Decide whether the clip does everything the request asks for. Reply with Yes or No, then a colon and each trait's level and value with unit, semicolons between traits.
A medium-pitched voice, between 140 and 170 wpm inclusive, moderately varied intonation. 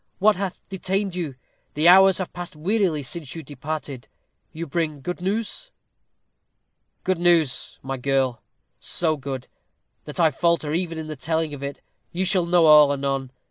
Yes: medium, 160 Hz; average, 160 wpm; average, 4.0 semitones